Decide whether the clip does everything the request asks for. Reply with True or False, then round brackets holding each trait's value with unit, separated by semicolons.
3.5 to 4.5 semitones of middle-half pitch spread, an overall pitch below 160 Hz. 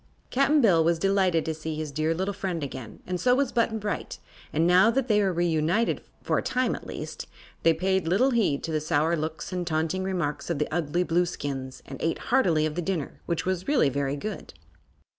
False (3.9 semitones; 170 Hz)